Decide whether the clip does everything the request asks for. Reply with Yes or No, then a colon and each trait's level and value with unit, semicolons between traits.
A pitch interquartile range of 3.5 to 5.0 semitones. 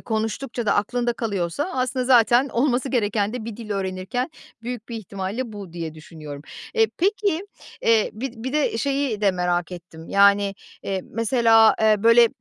Yes: average, 4.1 semitones